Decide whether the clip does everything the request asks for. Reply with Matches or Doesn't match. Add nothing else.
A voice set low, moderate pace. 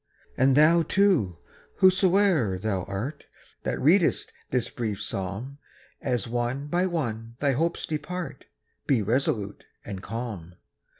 Doesn't match